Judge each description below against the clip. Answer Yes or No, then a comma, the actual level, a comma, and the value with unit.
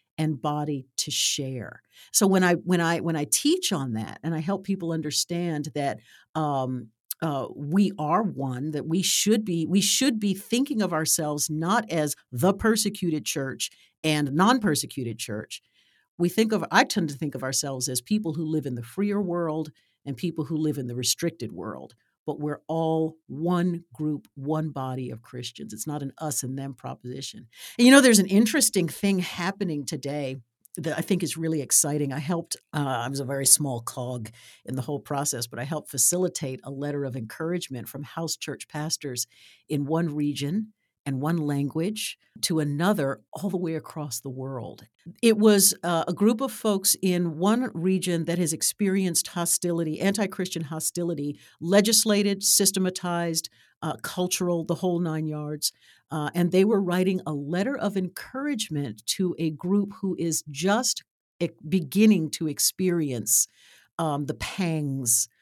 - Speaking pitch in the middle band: Yes, medium, 160 Hz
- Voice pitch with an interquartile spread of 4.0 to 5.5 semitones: Yes, average, 4.7 semitones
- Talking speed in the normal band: Yes, average, 170 wpm